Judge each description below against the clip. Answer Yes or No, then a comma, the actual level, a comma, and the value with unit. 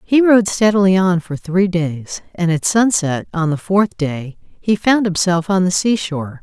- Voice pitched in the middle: Yes, medium, 180 Hz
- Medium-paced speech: Yes, average, 185 wpm